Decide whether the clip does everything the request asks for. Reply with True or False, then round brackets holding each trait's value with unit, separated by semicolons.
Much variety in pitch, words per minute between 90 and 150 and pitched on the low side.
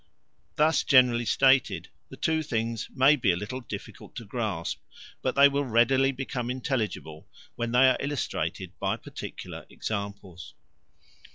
False (3.7 semitones; 140 wpm; 125 Hz)